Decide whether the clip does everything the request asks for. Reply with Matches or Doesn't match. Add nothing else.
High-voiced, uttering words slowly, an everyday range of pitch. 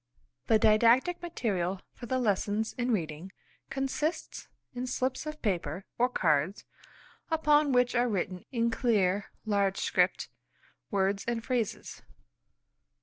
Matches